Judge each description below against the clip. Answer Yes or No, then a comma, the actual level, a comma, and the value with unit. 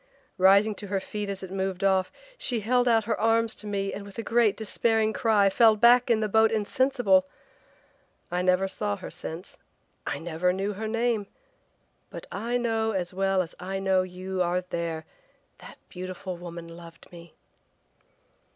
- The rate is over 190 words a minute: No, average, 170 wpm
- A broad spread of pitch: No, average, 3.3 semitones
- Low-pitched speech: No, high, 195 Hz